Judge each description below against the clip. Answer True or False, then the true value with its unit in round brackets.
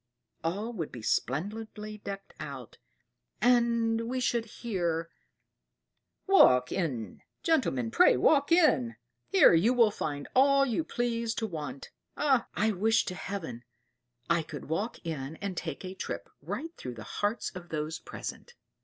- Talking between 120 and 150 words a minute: True (145 wpm)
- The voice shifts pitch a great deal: True (6.9 semitones)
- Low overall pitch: False (200 Hz)